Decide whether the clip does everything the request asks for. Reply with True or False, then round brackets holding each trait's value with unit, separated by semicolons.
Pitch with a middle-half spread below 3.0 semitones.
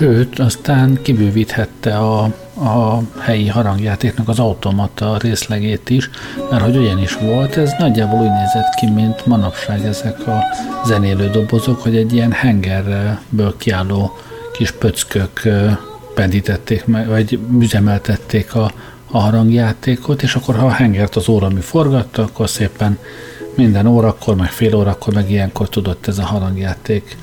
True (2.6 semitones)